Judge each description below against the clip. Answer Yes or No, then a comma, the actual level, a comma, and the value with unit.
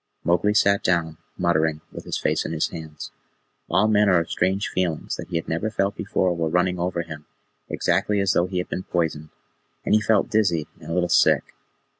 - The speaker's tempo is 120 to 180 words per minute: No, average, 200 wpm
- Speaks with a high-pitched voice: No, very low, 90 Hz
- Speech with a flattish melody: No, average, 3.1 semitones